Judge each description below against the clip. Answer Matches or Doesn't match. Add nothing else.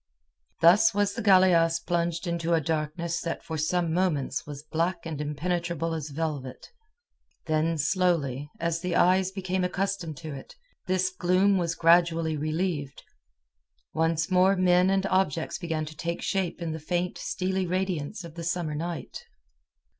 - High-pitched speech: Doesn't match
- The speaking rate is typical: Matches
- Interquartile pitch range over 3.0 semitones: Doesn't match